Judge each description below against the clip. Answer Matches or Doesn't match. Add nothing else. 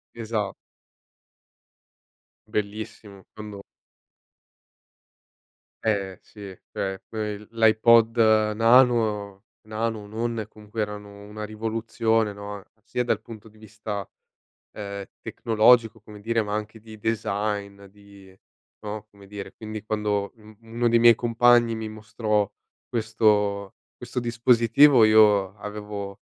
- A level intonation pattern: Matches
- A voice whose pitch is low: Matches